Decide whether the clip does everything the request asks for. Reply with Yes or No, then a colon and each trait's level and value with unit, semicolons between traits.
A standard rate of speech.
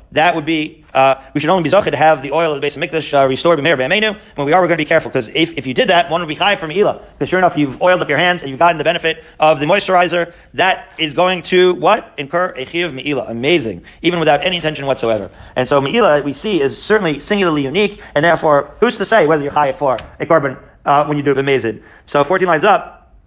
No: fast, 265 wpm